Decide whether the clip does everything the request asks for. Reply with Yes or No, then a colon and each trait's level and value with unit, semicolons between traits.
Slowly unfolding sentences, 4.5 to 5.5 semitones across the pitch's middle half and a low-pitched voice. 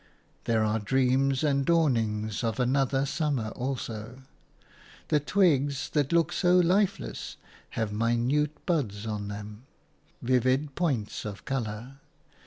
Yes: slow, 115 wpm; average, 4.8 semitones; low, 130 Hz